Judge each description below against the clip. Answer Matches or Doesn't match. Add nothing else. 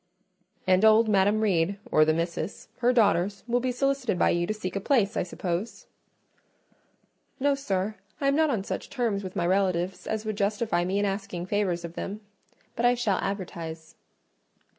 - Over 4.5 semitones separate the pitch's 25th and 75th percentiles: Doesn't match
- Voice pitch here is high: Matches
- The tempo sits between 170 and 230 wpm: Matches